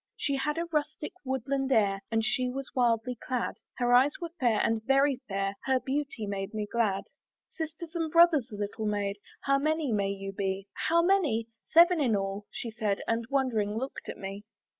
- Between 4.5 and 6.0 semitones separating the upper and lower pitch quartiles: Yes, wide, 5.5 semitones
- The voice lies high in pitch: Yes, high, 245 Hz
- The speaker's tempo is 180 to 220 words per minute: Yes, average, 185 wpm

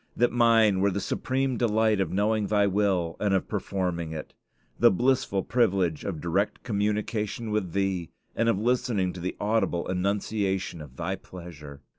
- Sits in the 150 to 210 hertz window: No, low, 100 Hz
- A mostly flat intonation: No, average, 3.2 semitones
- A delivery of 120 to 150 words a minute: No, average, 160 wpm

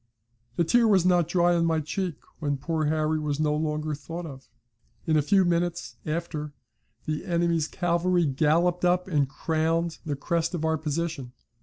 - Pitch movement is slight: Yes, narrow, 2.3 semitones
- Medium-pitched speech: Yes, medium, 160 Hz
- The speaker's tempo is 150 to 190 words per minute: Yes, average, 170 wpm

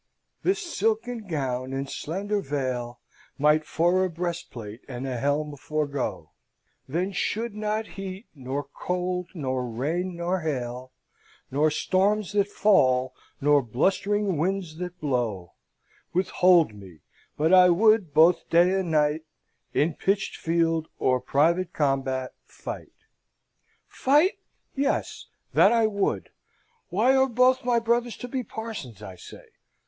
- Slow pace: Yes, slow, 130 wpm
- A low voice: No, medium, 170 Hz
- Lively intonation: Yes, wide, 6.8 semitones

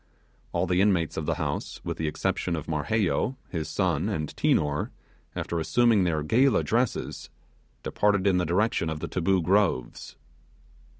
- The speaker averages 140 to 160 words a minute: Yes, average, 155 wpm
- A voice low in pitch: Yes, very low, 90 Hz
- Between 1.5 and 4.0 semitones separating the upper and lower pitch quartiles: No, average, 4.7 semitones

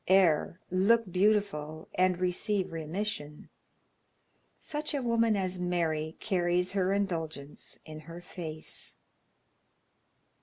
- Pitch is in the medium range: Yes, medium, 180 Hz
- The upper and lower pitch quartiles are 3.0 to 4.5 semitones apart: Yes, average, 3.8 semitones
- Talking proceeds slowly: Yes, slow, 100 wpm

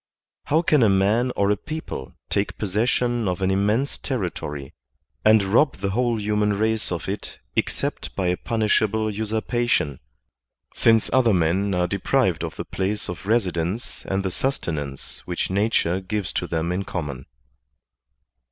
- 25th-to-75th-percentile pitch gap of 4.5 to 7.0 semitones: No, average, 3.7 semitones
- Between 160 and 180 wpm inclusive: No, average, 150 wpm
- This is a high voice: No, low, 100 Hz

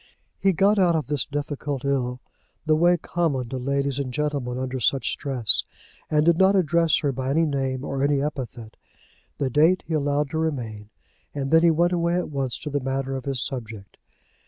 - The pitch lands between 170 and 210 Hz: No, medium, 140 Hz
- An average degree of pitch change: Yes, average, 3.5 semitones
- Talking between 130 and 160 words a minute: No, average, 195 wpm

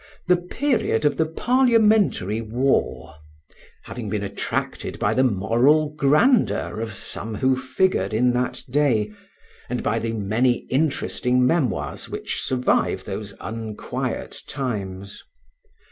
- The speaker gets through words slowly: Yes, slow, 115 wpm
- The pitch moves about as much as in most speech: No, wide, 5.8 semitones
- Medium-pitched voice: No, low, 125 Hz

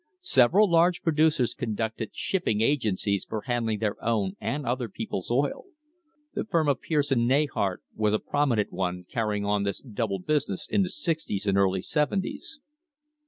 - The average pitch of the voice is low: Yes, low, 115 Hz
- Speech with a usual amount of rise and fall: No, wide, 6.4 semitones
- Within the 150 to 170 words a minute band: Yes, average, 160 wpm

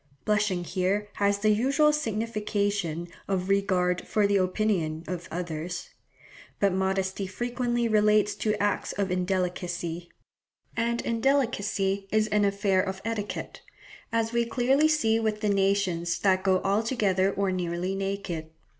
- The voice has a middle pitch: No, high, 200 Hz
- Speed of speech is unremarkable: No, slow, 130 wpm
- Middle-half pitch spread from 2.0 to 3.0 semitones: Yes, average, 2.7 semitones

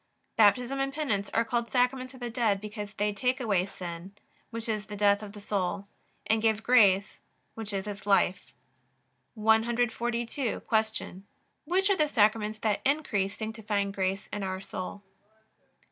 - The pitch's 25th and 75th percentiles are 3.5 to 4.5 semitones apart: No, average, 3.0 semitones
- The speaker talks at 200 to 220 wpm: No, average, 155 wpm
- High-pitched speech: Yes, high, 215 Hz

